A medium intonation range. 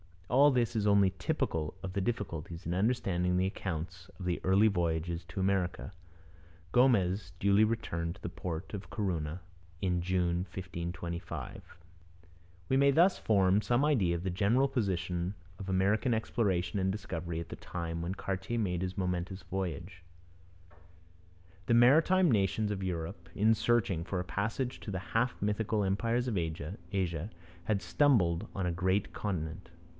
Yes: average, 3.6 semitones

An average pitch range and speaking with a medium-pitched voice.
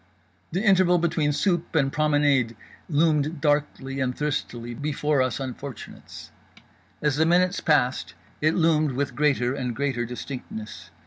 Yes: average, 3.2 semitones; medium, 145 Hz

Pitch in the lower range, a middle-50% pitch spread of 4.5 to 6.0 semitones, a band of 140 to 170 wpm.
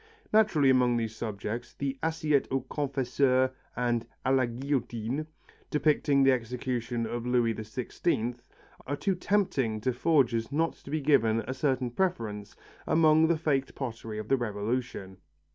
No: low, 130 Hz; average, 3.7 semitones; average, 145 wpm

